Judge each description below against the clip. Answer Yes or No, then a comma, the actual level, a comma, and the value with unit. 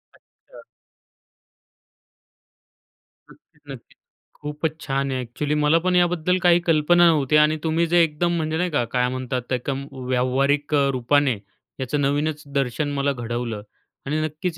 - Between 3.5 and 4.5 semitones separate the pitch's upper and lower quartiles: No, average, 3.1 semitones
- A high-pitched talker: No, medium, 145 Hz